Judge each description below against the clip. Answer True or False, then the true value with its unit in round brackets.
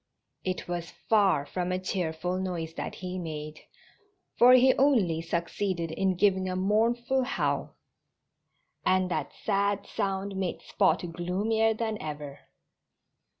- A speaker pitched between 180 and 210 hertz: True (185 Hz)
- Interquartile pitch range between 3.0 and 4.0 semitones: True (3.4 semitones)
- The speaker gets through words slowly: True (125 wpm)